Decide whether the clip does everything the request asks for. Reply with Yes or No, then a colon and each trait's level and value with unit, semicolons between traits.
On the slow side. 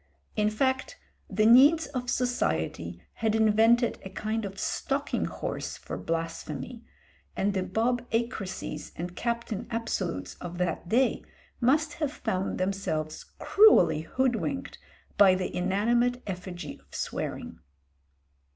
Yes: slow, 120 wpm